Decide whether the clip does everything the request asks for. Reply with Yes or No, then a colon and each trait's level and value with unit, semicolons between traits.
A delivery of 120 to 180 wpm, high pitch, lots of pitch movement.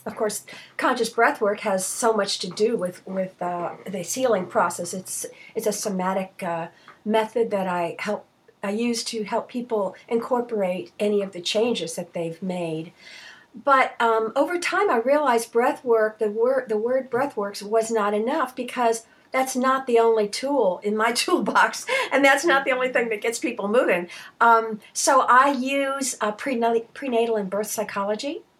No: average, 175 wpm; high, 225 Hz; average, 4.0 semitones